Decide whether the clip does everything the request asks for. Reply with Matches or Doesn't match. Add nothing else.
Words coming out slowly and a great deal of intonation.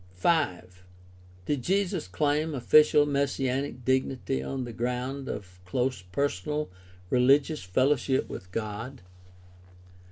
Doesn't match